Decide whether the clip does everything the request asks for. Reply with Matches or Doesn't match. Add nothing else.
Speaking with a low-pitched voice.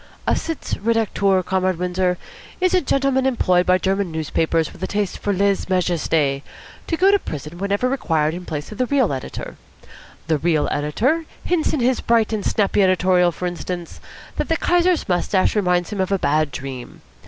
Doesn't match